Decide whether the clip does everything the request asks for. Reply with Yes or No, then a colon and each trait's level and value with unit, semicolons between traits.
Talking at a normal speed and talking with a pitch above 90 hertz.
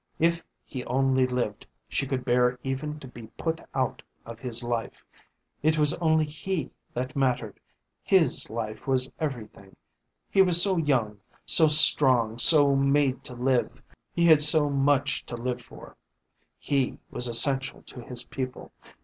Yes: average, 150 wpm; low, 135 Hz